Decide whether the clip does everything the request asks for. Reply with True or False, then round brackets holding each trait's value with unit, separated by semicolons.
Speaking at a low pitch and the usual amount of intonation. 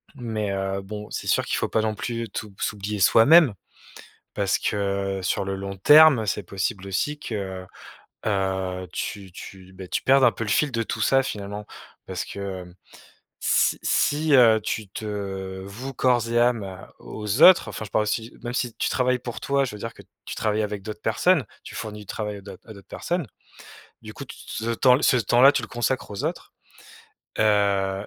True (105 Hz; 3.6 semitones)